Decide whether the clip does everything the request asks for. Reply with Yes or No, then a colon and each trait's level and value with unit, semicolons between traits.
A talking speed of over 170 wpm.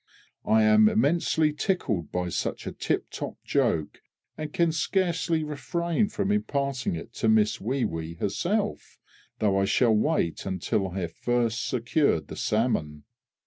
No: average, 145 wpm